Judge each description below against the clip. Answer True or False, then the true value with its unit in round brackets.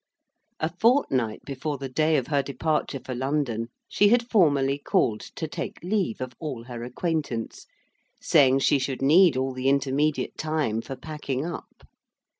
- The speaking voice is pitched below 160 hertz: True (140 Hz)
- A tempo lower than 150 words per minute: False (155 wpm)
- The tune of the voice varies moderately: True (3.5 semitones)